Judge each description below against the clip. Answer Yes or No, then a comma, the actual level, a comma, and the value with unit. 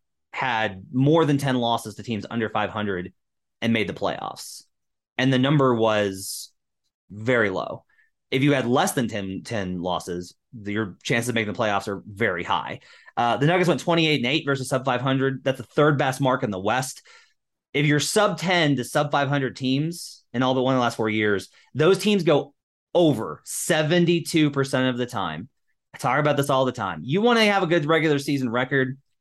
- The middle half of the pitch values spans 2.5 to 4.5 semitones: No, average, 5.2 semitones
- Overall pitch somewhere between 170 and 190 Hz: No, low, 130 Hz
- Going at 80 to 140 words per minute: No, fast, 205 wpm